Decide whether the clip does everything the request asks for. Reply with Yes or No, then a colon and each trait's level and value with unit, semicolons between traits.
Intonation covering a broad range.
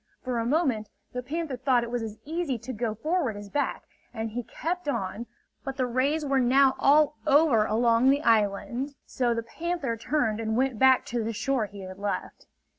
No: average, 3.9 semitones